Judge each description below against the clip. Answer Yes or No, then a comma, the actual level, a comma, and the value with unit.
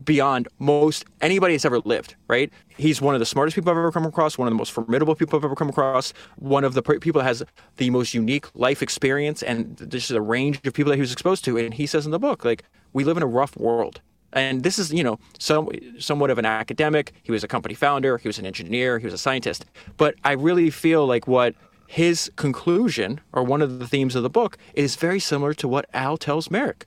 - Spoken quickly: Yes, fast, 245 wpm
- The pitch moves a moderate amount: Yes, average, 3.8 semitones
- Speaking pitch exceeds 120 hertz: Yes, medium, 140 Hz